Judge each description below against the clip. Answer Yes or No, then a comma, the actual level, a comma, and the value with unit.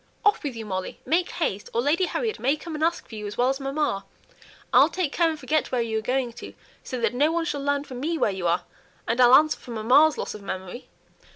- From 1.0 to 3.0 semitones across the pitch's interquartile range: No, wide, 5.4 semitones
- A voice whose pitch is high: Yes, very high, 270 Hz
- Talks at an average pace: No, fast, 255 wpm